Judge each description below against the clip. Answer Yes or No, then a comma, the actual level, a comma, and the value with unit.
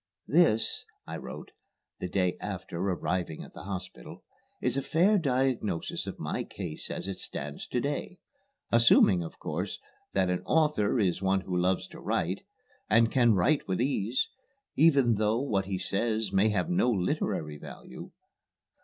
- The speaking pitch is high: No, low, 100 Hz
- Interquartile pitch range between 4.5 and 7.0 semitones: Yes, wide, 5.4 semitones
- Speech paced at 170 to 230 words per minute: No, average, 155 wpm